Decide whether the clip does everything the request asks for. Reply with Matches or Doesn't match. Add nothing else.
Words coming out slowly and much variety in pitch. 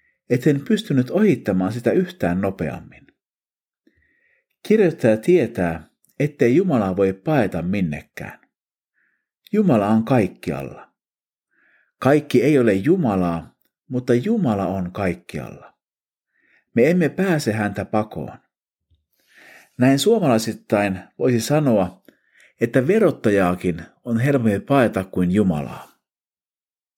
Matches